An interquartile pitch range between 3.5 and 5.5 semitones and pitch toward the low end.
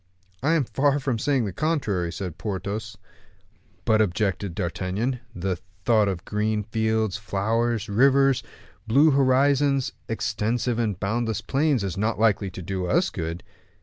Yes: average, 4.7 semitones; low, 110 Hz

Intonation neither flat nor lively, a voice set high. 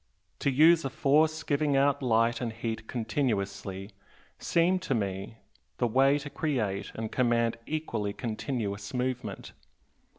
No: average, 4.6 semitones; low, 120 Hz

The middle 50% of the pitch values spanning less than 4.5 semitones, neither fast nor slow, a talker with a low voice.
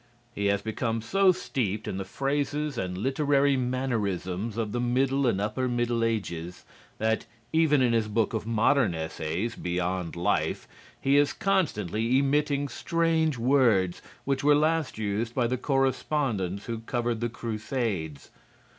No: average, 5.0 semitones; average, 145 wpm; low, 120 Hz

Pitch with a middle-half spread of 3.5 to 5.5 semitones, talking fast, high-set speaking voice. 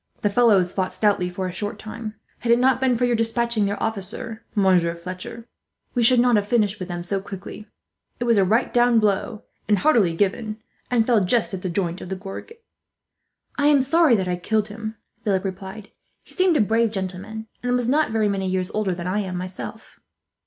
Yes: average, 3.8 semitones; fast, 210 wpm; high, 210 Hz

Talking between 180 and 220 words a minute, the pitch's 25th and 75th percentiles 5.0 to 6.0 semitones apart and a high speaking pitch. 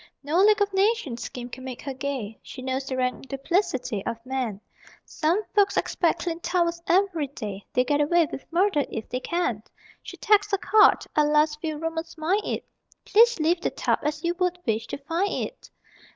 Yes: average, 190 wpm; wide, 5.6 semitones; very high, 310 Hz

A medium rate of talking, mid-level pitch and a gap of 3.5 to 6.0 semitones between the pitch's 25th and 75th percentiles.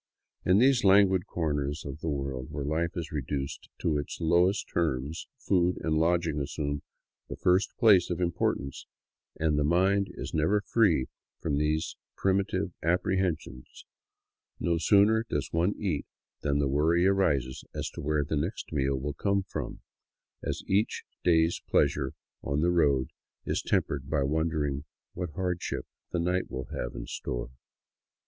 No: average, 150 wpm; very low, 80 Hz; average, 4.0 semitones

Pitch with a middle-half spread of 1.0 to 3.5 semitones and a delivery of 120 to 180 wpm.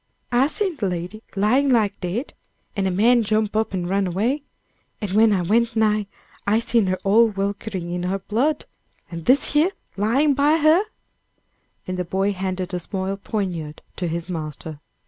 No: average, 4.1 semitones; average, 175 wpm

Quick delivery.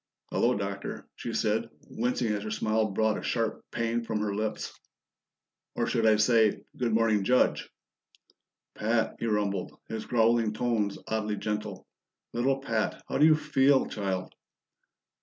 No: average, 145 wpm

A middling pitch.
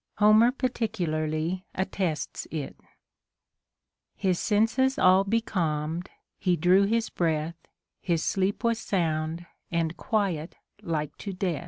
Yes: medium, 180 Hz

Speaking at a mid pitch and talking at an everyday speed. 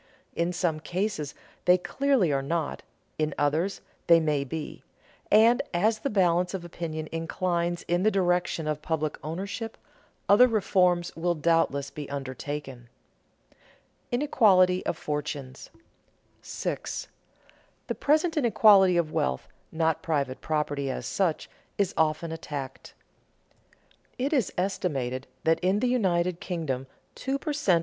No: medium, 170 Hz; slow, 130 wpm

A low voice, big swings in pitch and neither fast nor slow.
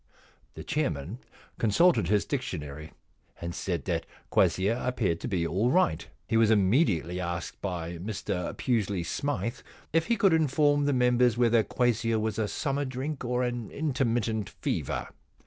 Yes: low, 115 Hz; wide, 6.0 semitones; average, 145 wpm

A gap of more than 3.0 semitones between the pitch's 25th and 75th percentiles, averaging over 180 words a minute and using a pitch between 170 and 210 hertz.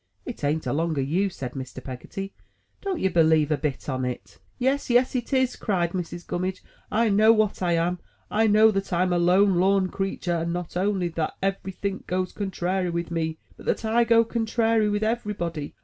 Yes: average, 4.1 semitones; average, 195 wpm; medium, 185 Hz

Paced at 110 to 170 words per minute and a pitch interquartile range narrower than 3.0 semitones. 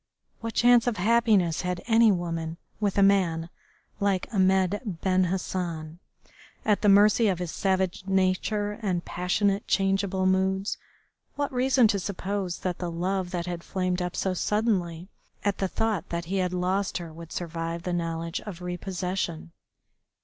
Yes: average, 155 wpm; narrow, 2.5 semitones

